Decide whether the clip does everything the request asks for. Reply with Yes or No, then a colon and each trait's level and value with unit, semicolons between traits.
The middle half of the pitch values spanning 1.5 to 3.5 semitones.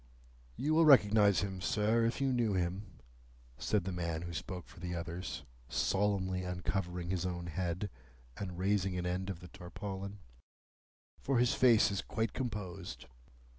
Yes: average, 2.8 semitones